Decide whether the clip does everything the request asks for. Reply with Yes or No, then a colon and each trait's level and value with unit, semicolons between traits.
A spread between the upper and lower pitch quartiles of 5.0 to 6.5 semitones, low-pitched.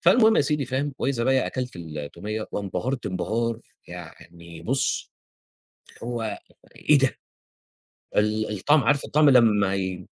Yes: wide, 5.5 semitones; low, 115 Hz